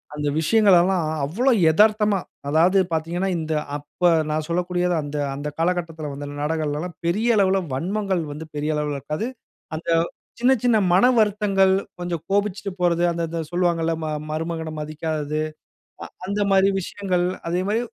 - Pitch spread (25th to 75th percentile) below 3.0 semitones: No, average, 3.8 semitones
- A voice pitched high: No, medium, 175 Hz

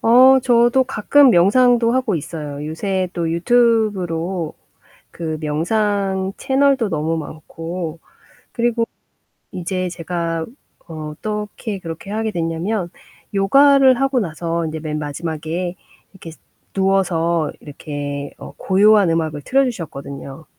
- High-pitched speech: No, medium, 180 Hz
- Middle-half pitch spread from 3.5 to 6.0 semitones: Yes, wide, 5.4 semitones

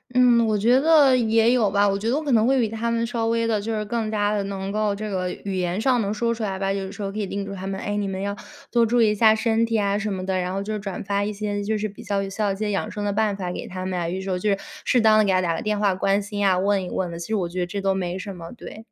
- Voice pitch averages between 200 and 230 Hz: Yes, high, 205 Hz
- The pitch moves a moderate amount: No, narrow, 2.3 semitones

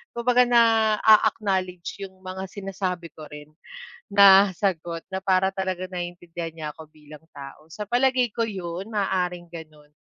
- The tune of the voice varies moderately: Yes, average, 3.3 semitones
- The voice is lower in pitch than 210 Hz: Yes, medium, 185 Hz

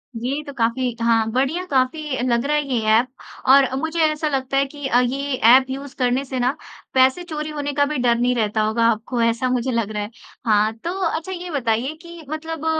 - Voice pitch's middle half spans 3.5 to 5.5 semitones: Yes, average, 4.0 semitones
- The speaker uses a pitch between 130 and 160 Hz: No, very high, 260 Hz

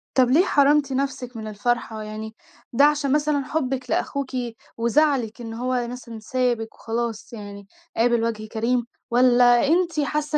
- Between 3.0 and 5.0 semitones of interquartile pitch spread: Yes, average, 3.6 semitones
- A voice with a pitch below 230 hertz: No, high, 245 Hz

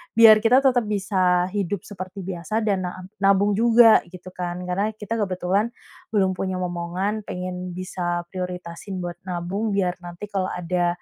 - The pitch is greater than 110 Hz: Yes, medium, 185 Hz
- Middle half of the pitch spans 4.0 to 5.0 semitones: No, narrow, 2.5 semitones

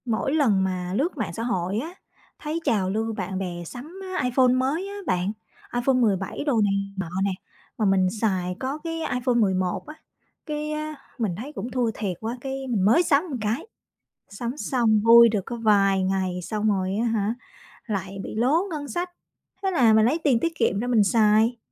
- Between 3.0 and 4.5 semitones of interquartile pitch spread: No, average, 5.2 semitones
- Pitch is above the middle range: Yes, high, 225 Hz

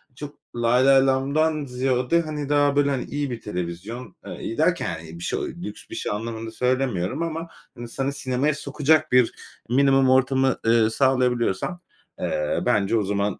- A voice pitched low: Yes, low, 130 Hz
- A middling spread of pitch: Yes, average, 3.5 semitones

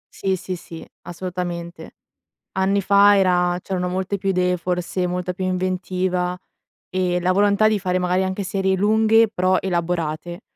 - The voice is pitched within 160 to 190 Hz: Yes, medium, 185 Hz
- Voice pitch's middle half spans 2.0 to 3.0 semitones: No, narrow, 1.3 semitones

